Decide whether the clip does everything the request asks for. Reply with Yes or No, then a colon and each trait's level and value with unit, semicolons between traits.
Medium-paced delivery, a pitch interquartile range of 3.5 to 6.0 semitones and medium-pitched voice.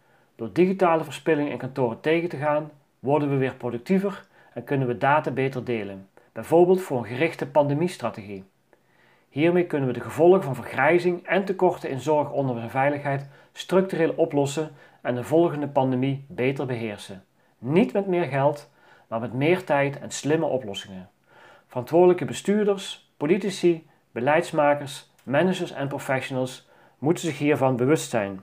Yes: average, 145 wpm; average, 5.0 semitones; medium, 145 Hz